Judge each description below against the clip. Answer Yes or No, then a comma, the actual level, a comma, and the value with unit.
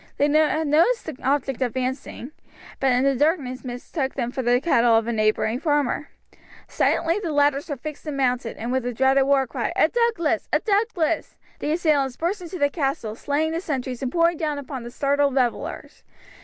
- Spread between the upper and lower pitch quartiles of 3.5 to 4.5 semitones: Yes, average, 3.8 semitones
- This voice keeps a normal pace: Yes, average, 190 wpm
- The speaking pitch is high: Yes, very high, 280 Hz